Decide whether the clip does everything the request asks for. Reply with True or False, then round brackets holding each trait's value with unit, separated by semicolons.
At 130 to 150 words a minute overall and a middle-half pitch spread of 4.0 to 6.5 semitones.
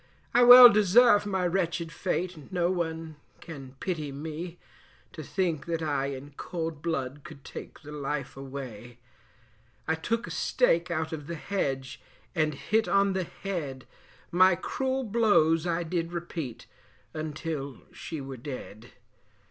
True (140 wpm; 4.4 semitones)